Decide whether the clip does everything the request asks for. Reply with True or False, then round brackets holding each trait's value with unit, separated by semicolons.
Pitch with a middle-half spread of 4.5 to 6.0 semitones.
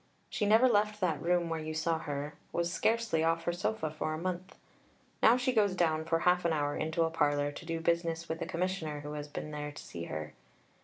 False (2.9 semitones)